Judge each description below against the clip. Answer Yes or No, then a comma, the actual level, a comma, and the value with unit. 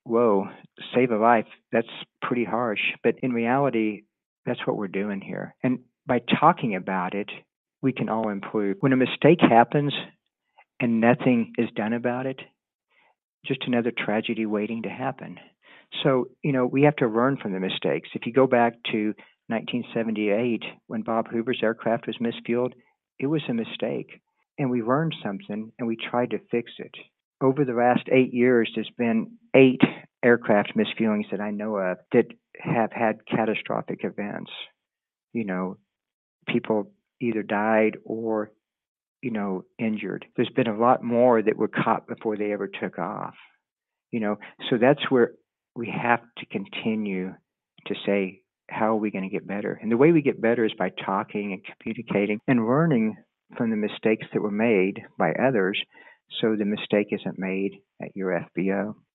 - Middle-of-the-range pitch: No, low, 115 Hz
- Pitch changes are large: No, average, 3.1 semitones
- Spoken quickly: No, average, 165 wpm